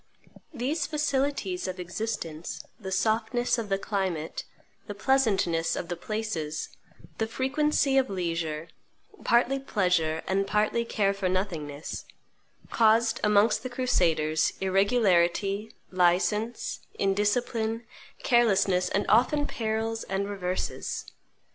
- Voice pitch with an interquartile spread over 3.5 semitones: Yes, average, 4.4 semitones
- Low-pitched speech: No, high, 205 Hz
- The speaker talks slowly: Yes, slow, 105 wpm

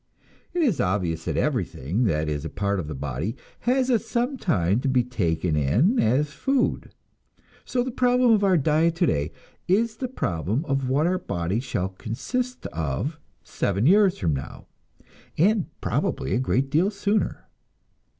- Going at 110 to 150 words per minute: No, average, 160 wpm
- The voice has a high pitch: No, low, 135 Hz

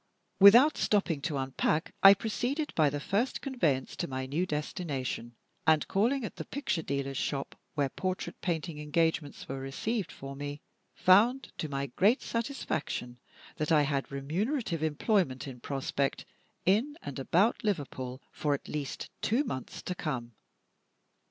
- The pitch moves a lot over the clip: Yes, wide, 6.8 semitones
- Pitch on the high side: No, medium, 155 Hz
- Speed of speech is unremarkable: Yes, average, 145 wpm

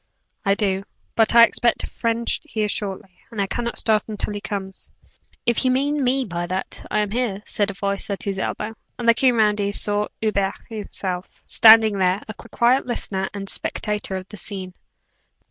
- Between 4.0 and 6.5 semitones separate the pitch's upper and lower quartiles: No, average, 2.9 semitones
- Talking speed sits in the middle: Yes, average, 180 wpm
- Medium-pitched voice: No, high, 210 Hz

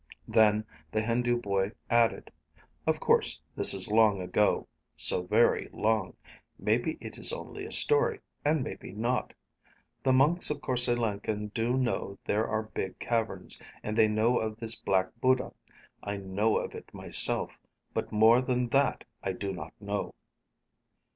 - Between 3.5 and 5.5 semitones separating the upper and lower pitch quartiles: No, average, 3.0 semitones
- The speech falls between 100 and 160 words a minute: Yes, average, 155 wpm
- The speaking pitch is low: Yes, low, 110 Hz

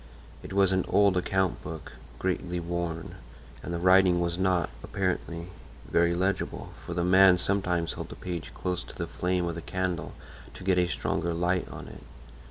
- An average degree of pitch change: No, narrow, 1.3 semitones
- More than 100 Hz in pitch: No, very low, 90 Hz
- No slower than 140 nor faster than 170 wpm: No, average, 180 wpm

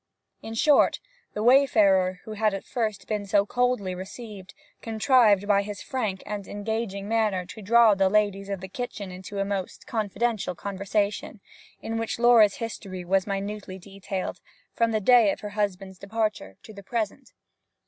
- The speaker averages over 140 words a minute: Yes, average, 160 wpm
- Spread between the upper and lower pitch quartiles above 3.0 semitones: No, narrow, 2.4 semitones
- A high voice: Yes, high, 205 Hz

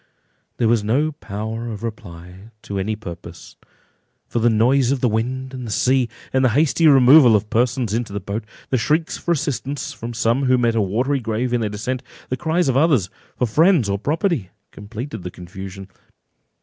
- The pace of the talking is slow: No, average, 180 wpm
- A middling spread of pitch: Yes, average, 3.9 semitones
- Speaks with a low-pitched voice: Yes, low, 120 Hz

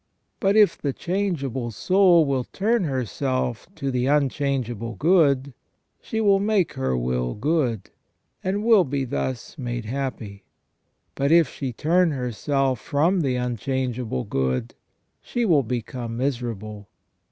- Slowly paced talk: Yes, slow, 130 wpm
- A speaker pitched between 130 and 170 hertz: Yes, low, 135 Hz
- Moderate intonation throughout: No, wide, 5.8 semitones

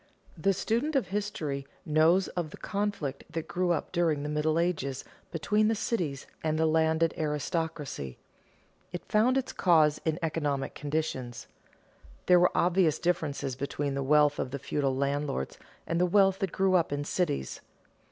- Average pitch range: Yes, average, 3.8 semitones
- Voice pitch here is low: No, medium, 160 Hz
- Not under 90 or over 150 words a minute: No, average, 160 wpm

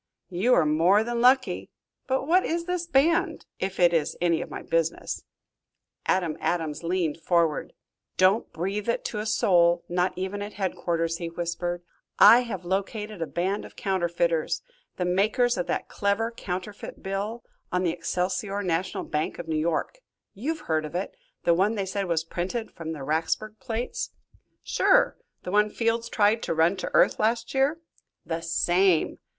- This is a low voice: No, high, 190 Hz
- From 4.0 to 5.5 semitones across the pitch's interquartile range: Yes, average, 4.7 semitones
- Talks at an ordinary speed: Yes, average, 165 wpm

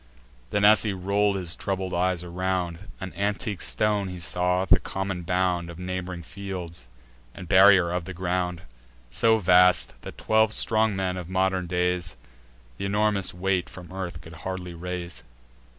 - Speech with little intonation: Yes, narrow, 1.7 semitones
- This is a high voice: No, very low, 90 Hz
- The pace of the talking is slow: No, average, 155 wpm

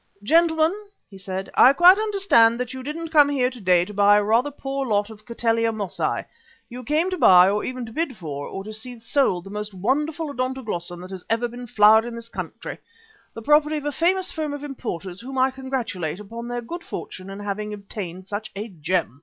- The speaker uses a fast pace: Yes, fast, 210 wpm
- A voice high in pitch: Yes, high, 230 Hz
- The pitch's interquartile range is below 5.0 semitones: No, wide, 5.5 semitones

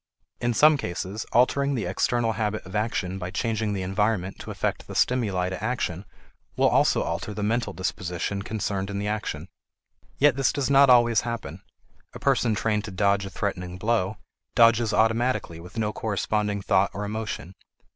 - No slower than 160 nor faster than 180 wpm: Yes, average, 170 wpm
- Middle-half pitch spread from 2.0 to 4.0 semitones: Yes, average, 3.3 semitones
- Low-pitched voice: Yes, low, 105 Hz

